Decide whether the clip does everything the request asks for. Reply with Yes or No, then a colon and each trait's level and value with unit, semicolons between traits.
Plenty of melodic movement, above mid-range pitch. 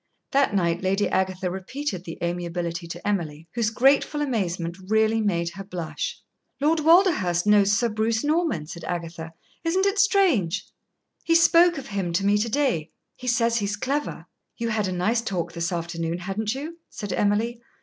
Yes: wide, 7.3 semitones; high, 205 Hz